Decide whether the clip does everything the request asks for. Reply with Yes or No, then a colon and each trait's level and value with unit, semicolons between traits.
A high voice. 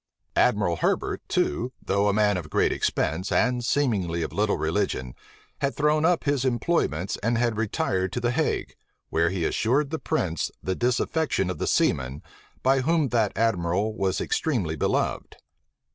No: low, 110 Hz